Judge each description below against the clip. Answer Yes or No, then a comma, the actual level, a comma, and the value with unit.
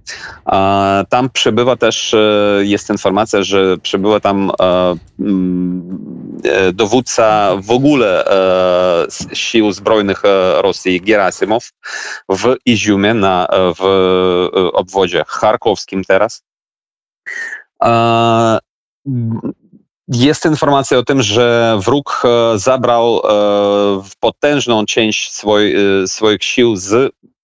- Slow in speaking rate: Yes, slow, 70 wpm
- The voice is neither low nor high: No, low, 105 Hz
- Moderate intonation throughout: Yes, average, 3.3 semitones